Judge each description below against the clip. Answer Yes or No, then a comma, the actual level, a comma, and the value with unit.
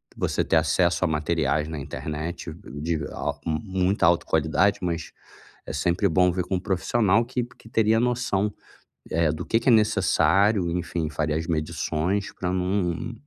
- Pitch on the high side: No, very low, 90 Hz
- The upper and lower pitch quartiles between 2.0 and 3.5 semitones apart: No, average, 4.2 semitones